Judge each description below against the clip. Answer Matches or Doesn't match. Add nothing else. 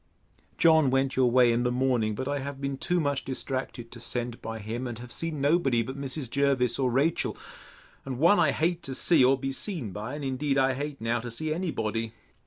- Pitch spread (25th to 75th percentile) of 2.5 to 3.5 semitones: Matches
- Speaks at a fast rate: Matches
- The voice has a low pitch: Matches